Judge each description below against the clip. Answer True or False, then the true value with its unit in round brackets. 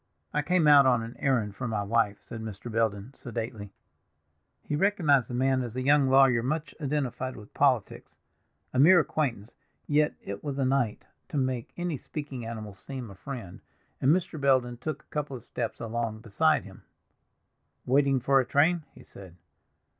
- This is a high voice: False (130 Hz)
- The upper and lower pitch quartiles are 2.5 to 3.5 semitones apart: False (4.0 semitones)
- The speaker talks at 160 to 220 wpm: True (175 wpm)